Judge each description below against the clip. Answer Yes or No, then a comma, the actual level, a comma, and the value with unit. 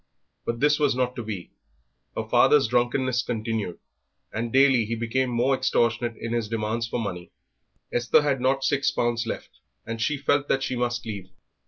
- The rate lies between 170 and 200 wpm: Yes, average, 175 wpm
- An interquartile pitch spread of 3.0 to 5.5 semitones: No, narrow, 2.5 semitones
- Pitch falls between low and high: No, low, 120 Hz